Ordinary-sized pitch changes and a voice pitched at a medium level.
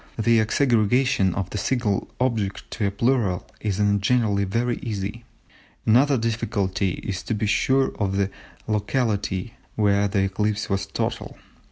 No: average, 3.0 semitones; low, 105 Hz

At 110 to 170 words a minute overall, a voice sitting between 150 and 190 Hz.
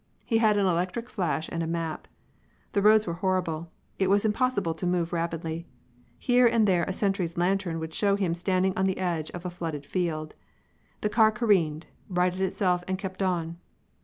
No: average, 185 wpm; medium, 185 Hz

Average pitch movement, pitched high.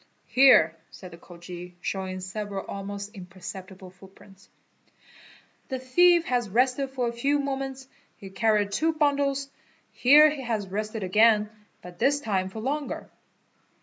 No: wide, 6.0 semitones; high, 215 Hz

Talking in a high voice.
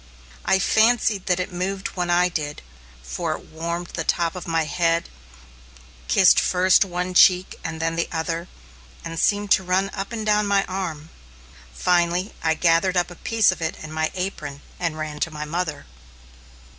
No: medium, 175 Hz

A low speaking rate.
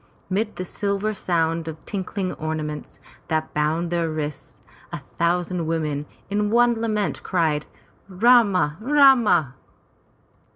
Yes: slow, 120 wpm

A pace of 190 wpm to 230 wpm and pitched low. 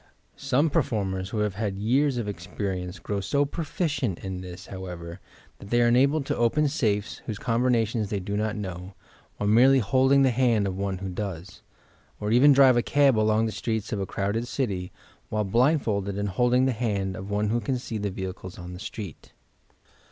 Yes: average, 195 wpm; low, 105 Hz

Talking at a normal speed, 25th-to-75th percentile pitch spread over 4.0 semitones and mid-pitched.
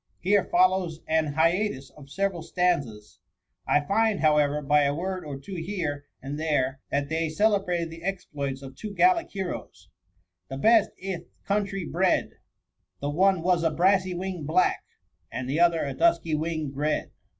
Yes: average, 175 wpm; average, 4.6 semitones; medium, 165 Hz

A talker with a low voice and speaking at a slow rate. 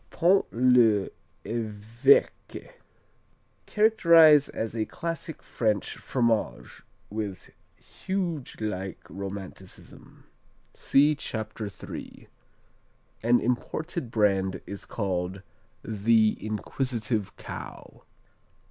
Yes: low, 110 Hz; slow, 75 wpm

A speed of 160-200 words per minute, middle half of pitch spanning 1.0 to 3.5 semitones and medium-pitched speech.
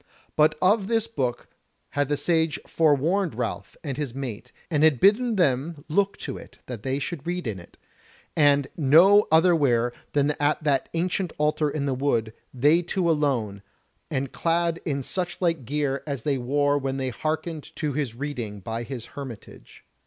No: average, 170 wpm; average, 3.9 semitones; medium, 145 Hz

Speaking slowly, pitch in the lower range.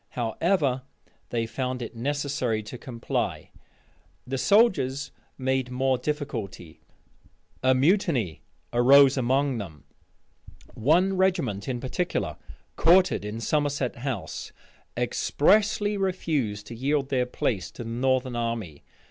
Yes: slow, 110 wpm; low, 130 Hz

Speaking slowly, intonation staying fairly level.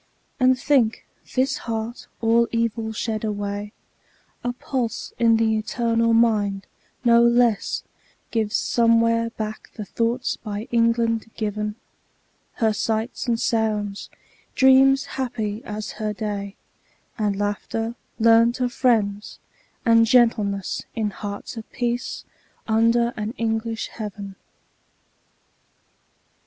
Yes: slow, 110 wpm; narrow, 1.9 semitones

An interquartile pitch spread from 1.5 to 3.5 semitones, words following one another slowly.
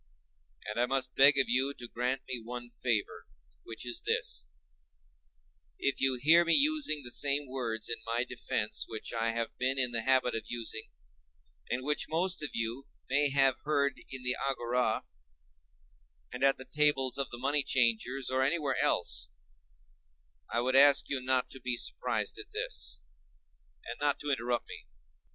No: average, 2.8 semitones; average, 165 wpm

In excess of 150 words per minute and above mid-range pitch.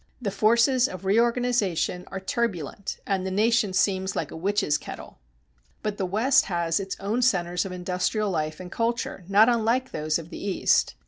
Yes: average, 175 wpm; high, 195 Hz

